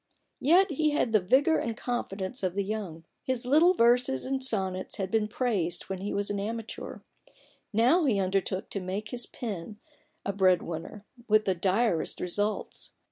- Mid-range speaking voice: No, high, 210 Hz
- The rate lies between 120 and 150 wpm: No, average, 195 wpm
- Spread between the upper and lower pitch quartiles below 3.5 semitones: No, average, 4.5 semitones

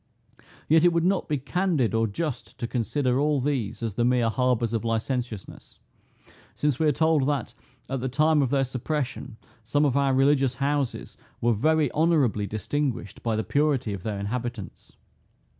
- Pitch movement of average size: Yes, average, 4.1 semitones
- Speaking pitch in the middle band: No, low, 130 Hz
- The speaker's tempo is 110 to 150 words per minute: No, average, 170 wpm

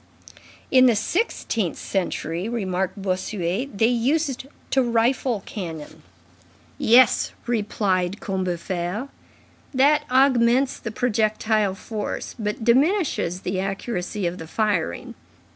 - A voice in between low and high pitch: No, high, 215 Hz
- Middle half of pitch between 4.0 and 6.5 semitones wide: Yes, average, 4.8 semitones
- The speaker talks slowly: Yes, slow, 100 wpm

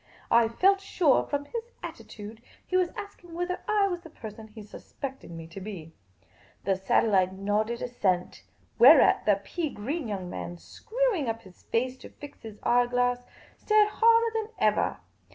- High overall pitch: Yes, high, 245 Hz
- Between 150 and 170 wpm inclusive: Yes, average, 165 wpm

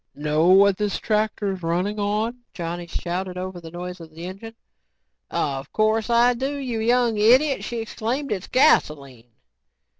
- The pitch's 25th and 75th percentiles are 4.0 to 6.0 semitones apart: Yes, average, 4.9 semitones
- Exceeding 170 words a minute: No, average, 150 wpm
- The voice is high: Yes, high, 205 Hz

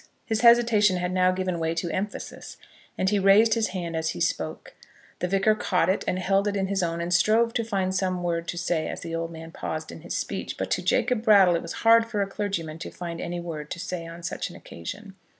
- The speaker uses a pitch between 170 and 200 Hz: Yes, medium, 185 Hz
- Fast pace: Yes, fast, 240 wpm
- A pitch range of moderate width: Yes, average, 3.5 semitones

